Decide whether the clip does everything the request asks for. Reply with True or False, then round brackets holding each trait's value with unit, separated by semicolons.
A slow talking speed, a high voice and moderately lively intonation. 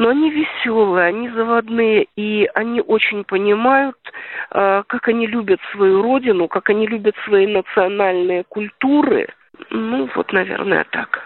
False (130 wpm; 215 Hz; 3.2 semitones)